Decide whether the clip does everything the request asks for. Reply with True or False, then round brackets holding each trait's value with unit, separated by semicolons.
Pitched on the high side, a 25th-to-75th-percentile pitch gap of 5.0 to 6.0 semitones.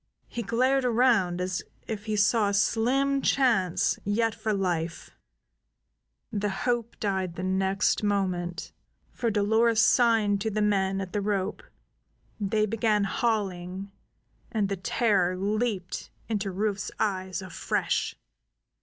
False (205 Hz; 2.8 semitones)